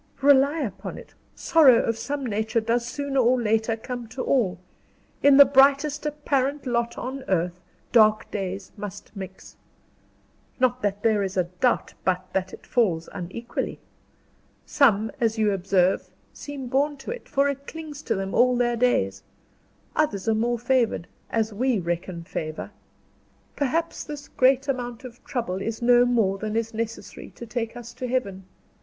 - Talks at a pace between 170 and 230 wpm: No, average, 160 wpm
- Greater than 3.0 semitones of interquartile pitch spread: Yes, average, 4.7 semitones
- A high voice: Yes, high, 235 Hz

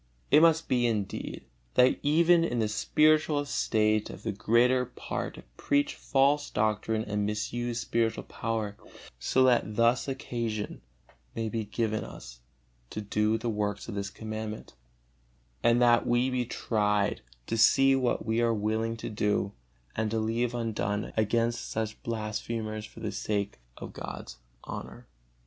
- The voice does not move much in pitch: Yes, narrow, 2.2 semitones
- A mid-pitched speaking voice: No, low, 115 Hz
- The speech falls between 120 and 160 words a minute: Yes, average, 145 wpm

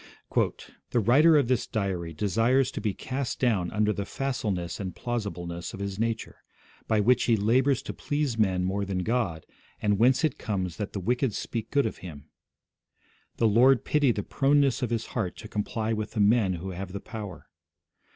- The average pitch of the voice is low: Yes, low, 110 Hz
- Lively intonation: No, average, 4.2 semitones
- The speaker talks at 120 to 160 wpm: No, average, 185 wpm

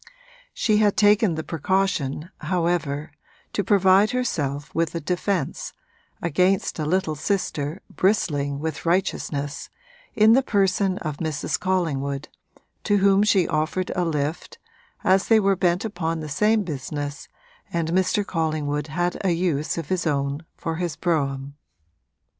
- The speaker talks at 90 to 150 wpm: Yes, slow, 135 wpm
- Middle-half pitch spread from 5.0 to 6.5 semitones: No, average, 4.4 semitones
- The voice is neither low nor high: Yes, medium, 170 Hz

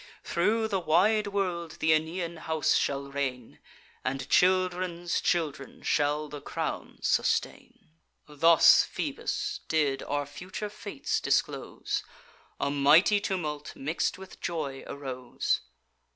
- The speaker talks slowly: Yes, slow, 110 wpm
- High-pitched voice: No, medium, 160 Hz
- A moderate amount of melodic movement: Yes, average, 4.4 semitones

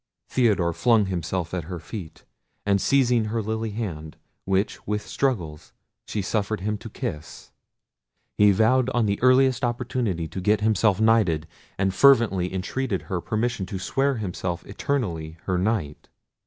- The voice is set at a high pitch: No, low, 105 Hz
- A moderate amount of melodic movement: Yes, average, 4.4 semitones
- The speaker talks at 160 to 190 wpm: No, average, 145 wpm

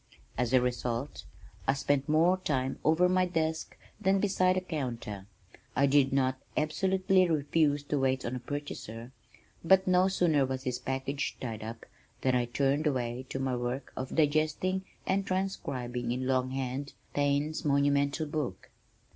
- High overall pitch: No, medium, 140 Hz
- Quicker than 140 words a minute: Yes, average, 155 wpm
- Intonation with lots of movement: No, average, 3.9 semitones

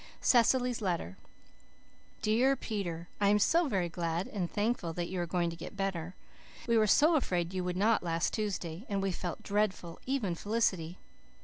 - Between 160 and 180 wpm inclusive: Yes, average, 175 wpm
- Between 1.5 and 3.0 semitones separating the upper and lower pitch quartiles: No, average, 4.0 semitones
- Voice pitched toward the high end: Yes, high, 195 Hz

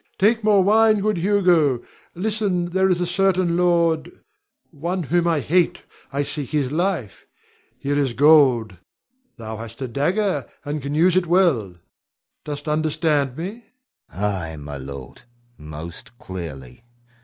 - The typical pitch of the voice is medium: Yes, medium, 155 Hz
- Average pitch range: No, wide, 7.3 semitones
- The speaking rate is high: No, average, 140 wpm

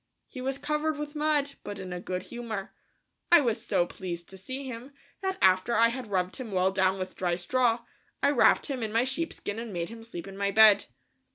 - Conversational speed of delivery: No, fast, 215 wpm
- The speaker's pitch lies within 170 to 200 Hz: No, high, 225 Hz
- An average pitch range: No, wide, 5.8 semitones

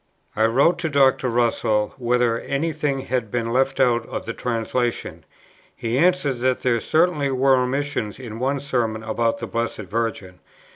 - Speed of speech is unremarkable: Yes, average, 165 wpm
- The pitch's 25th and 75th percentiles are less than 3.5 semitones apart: Yes, average, 3.0 semitones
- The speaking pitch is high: No, low, 125 Hz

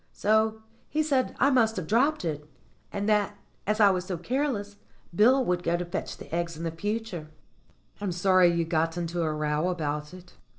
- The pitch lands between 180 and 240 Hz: Yes, medium, 185 Hz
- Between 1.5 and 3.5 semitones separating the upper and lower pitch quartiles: No, average, 4.5 semitones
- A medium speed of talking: Yes, average, 185 wpm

